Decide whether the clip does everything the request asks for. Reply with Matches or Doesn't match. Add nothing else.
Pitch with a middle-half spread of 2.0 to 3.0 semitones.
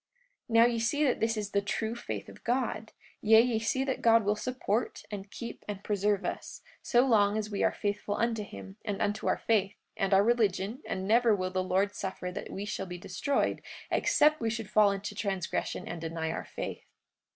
Matches